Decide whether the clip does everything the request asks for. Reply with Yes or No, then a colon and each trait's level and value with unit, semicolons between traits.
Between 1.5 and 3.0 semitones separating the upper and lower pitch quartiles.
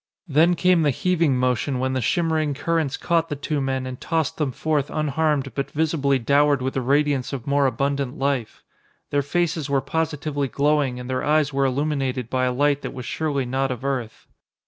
Yes: narrow, 2.6 semitones